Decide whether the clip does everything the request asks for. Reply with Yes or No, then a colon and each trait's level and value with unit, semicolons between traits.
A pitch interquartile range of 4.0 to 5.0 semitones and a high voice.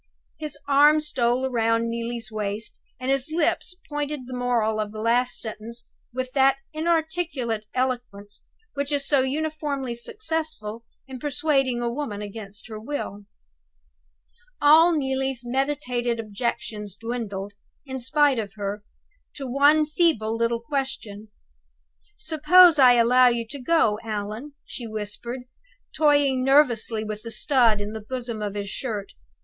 Yes: average, 4.5 semitones; high, 245 Hz